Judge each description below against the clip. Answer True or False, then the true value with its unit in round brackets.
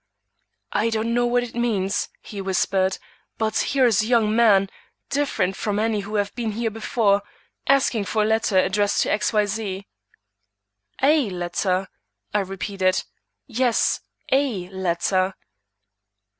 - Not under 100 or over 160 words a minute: True (140 wpm)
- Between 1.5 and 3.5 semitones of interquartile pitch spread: True (3.0 semitones)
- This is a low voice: False (210 Hz)